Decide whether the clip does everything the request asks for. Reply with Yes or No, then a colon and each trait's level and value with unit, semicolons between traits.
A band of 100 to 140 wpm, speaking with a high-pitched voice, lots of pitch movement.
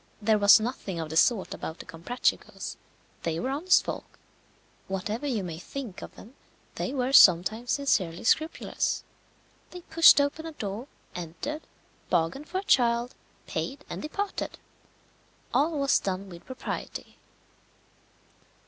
Yes: slow, 135 wpm; high, 235 Hz; wide, 7.4 semitones